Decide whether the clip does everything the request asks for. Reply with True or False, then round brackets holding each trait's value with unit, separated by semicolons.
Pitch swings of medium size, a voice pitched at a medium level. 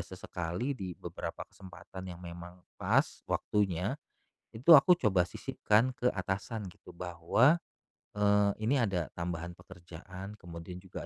False (3.2 semitones; 95 Hz)